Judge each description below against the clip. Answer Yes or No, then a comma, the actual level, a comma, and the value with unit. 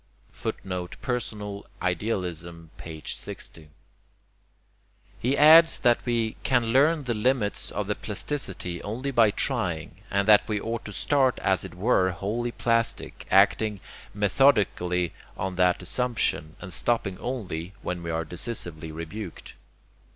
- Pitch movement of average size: Yes, average, 5.0 semitones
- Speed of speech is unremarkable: No, slow, 130 wpm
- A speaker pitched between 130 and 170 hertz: No, low, 105 Hz